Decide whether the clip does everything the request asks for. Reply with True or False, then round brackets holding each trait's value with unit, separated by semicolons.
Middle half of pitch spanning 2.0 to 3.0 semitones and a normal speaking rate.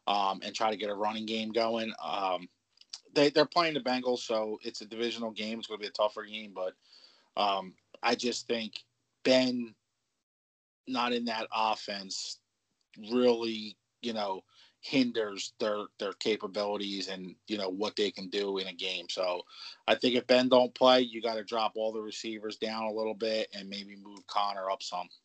True (2.6 semitones; 185 wpm)